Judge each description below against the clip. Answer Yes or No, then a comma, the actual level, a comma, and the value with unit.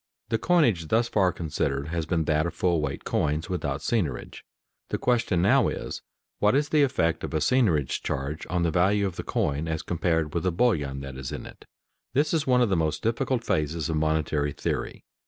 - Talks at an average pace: No, fast, 210 wpm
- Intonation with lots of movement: Yes, wide, 5.9 semitones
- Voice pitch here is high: No, very low, 85 Hz